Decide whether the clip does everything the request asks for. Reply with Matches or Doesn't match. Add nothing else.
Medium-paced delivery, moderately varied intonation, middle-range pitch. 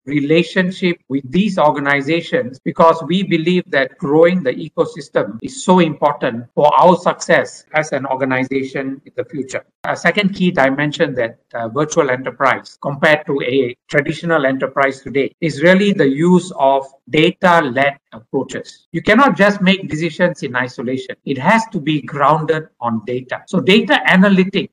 Matches